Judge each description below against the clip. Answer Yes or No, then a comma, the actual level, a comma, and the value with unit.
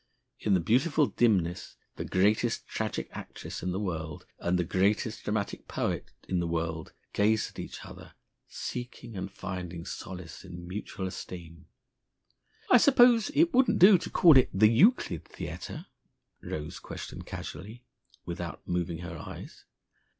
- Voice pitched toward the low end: Yes, very low, 95 Hz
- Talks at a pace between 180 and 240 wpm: No, average, 145 wpm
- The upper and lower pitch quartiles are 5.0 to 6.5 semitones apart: Yes, wide, 5.5 semitones